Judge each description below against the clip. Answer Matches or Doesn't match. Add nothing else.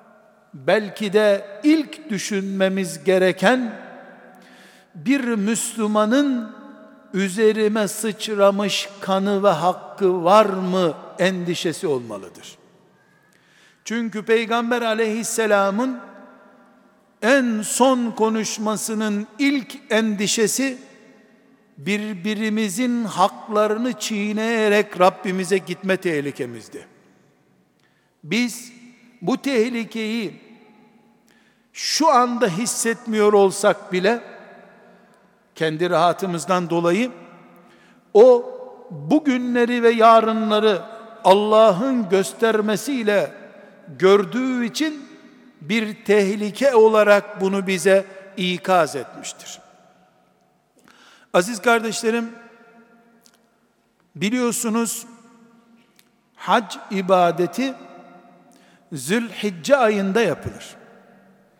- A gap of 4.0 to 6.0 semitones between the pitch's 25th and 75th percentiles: Doesn't match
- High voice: Matches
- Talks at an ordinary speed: Doesn't match